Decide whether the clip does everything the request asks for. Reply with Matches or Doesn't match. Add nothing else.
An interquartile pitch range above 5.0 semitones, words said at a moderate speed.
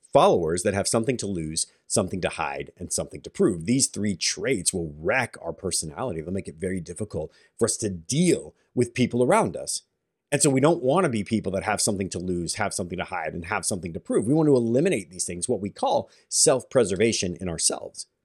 Doesn't match